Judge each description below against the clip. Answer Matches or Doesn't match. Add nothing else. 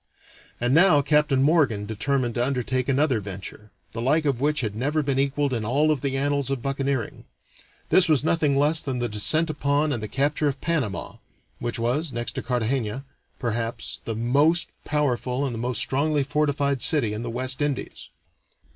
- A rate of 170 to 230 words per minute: Matches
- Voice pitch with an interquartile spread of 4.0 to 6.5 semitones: Doesn't match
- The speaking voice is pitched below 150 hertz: Matches